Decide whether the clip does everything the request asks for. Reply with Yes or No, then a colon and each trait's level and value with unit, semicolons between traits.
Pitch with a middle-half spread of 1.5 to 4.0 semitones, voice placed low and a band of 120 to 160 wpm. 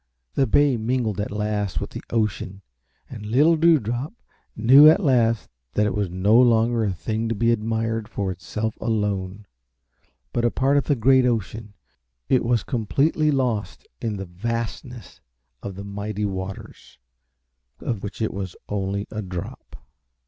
Yes: average, 3.1 semitones; low, 110 Hz; average, 155 wpm